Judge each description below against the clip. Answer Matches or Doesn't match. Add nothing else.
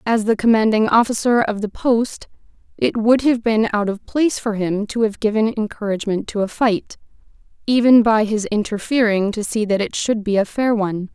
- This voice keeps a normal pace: Matches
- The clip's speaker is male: Doesn't match